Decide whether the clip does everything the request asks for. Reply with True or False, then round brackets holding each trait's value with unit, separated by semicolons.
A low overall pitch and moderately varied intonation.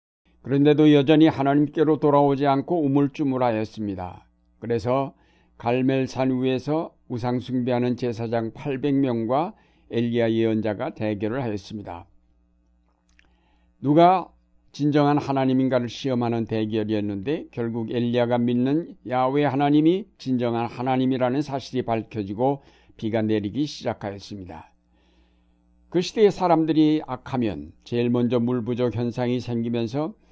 True (125 Hz; 4.4 semitones)